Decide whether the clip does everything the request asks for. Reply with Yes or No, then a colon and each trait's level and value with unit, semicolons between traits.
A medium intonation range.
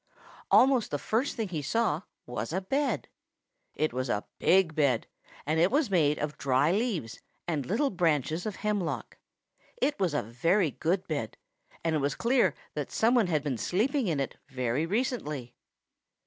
No: wide, 7.1 semitones